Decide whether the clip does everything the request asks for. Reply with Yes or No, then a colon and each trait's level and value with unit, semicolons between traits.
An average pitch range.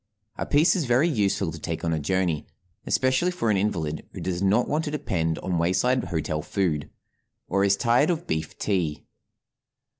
No: wide, 7.7 semitones